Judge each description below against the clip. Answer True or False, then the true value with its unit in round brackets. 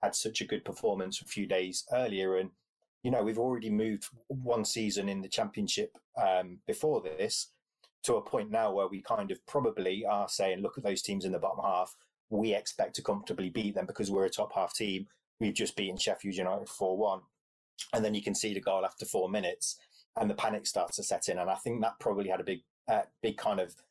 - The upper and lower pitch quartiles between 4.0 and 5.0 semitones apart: True (4.5 semitones)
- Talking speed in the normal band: False (225 wpm)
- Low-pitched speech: True (110 Hz)